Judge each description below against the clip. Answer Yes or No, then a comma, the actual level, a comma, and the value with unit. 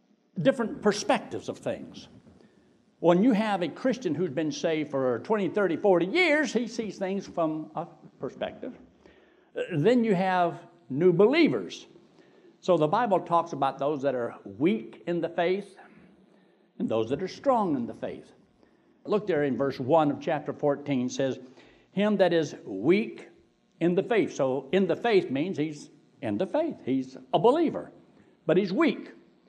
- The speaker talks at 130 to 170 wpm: Yes, average, 165 wpm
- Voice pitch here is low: No, medium, 185 Hz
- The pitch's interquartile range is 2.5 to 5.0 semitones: No, wide, 5.5 semitones